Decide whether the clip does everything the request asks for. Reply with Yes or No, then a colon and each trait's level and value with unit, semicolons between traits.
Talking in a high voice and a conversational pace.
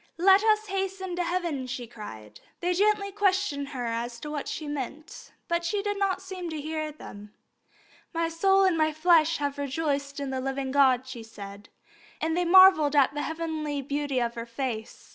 Yes: very high, 305 Hz; average, 185 wpm